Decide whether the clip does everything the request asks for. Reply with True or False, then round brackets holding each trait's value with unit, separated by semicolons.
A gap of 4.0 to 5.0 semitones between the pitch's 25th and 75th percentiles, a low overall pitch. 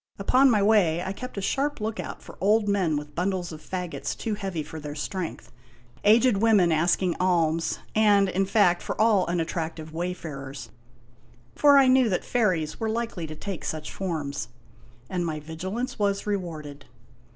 False (4.7 semitones; 185 Hz)